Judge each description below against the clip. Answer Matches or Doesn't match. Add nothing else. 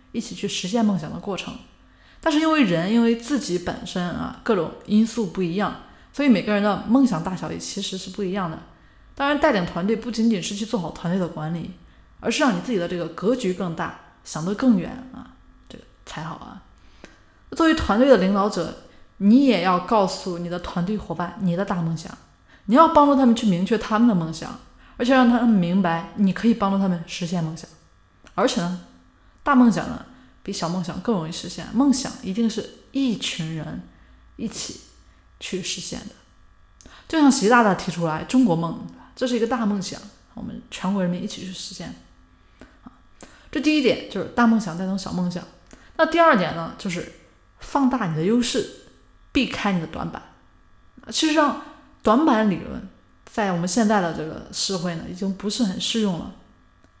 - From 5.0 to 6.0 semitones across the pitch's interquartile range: Matches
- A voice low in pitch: Doesn't match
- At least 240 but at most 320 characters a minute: Matches